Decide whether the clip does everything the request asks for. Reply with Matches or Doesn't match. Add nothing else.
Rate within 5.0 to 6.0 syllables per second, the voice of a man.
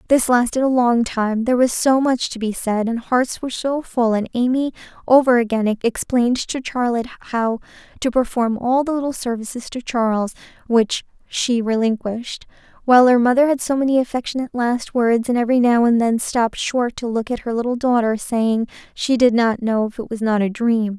Doesn't match